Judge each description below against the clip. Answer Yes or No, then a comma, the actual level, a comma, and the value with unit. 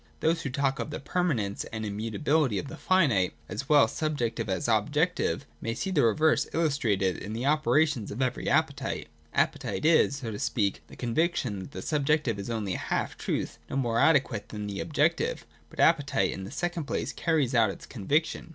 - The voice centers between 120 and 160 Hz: Yes, low, 135 Hz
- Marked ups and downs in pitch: Yes, wide, 6.3 semitones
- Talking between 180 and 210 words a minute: Yes, average, 190 wpm